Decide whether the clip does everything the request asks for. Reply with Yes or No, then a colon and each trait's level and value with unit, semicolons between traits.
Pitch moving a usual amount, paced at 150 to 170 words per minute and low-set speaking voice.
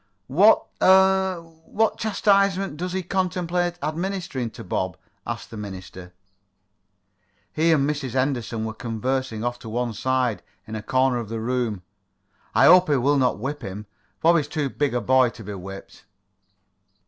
No: wide, 7.4 semitones; average, 160 wpm; low, 130 Hz